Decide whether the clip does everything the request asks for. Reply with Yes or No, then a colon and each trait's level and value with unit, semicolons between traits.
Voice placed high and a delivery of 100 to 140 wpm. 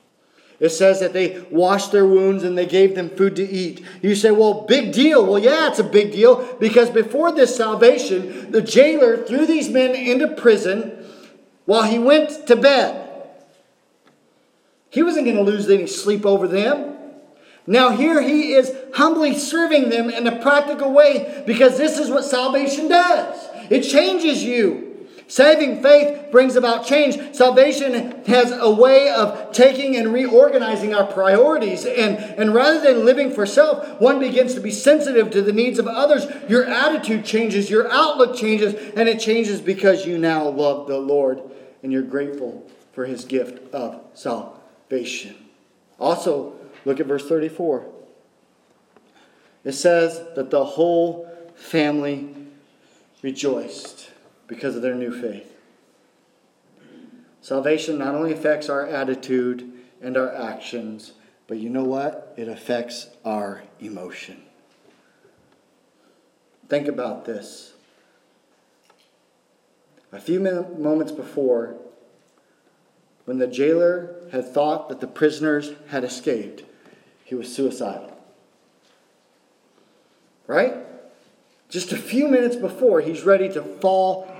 Yes: high, 210 Hz; slow, 135 wpm